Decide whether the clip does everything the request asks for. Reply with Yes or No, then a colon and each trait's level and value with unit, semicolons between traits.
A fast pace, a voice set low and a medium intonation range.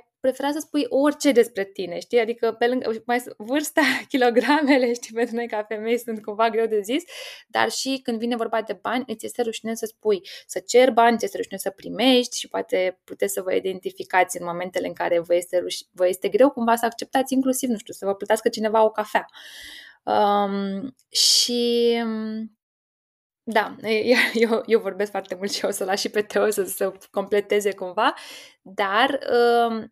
No: fast, 175 wpm; high, 230 Hz; average, 3.4 semitones